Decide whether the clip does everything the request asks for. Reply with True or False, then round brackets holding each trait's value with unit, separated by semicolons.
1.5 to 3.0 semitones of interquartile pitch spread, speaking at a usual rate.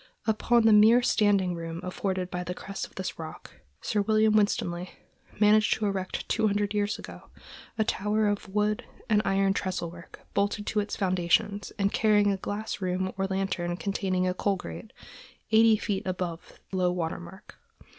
True (2.4 semitones; 170 wpm)